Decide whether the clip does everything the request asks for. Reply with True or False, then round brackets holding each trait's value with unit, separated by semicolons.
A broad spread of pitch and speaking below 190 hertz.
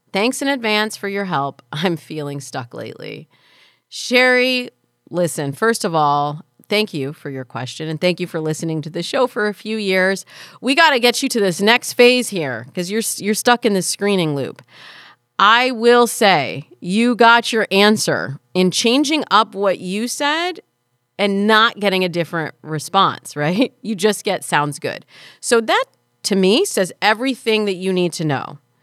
False (6.5 semitones; 195 Hz)